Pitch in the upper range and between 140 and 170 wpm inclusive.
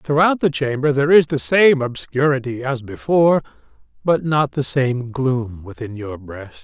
No: low, 135 Hz; average, 165 wpm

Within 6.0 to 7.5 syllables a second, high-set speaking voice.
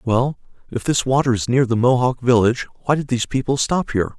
No: 6.2 syllables/s; low, 125 Hz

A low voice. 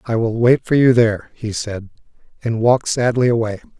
Yes: low, 115 Hz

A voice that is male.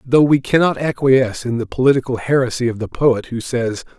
Yes: male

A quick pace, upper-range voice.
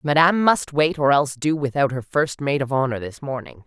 No: fast, 230 wpm; medium, 140 Hz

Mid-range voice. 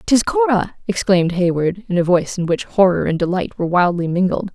Yes: medium, 180 Hz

